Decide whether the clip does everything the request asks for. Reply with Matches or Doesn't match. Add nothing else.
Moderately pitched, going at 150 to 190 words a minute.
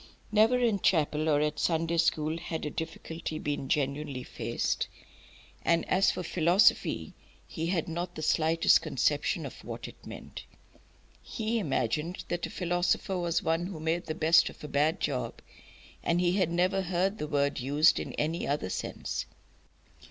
Matches